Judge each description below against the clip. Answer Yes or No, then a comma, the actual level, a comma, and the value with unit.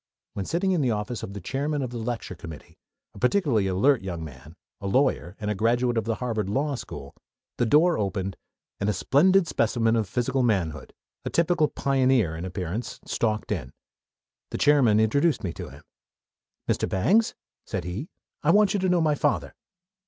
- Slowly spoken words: No, average, 180 wpm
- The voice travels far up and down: Yes, wide, 6.9 semitones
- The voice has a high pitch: No, low, 115 Hz